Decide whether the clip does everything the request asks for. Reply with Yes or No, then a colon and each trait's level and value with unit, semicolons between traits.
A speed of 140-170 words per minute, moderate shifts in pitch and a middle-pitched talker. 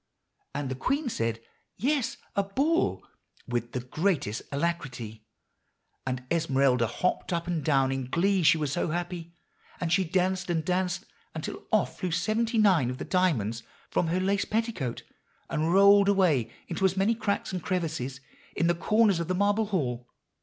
No: average, 165 wpm; wide, 6.5 semitones; medium, 170 Hz